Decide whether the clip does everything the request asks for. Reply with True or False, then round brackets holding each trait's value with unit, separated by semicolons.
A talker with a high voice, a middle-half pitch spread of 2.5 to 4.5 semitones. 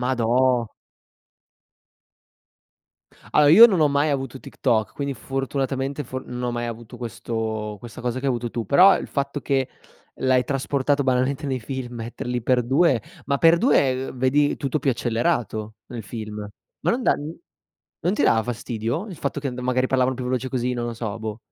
False (130 Hz; 2.8 semitones)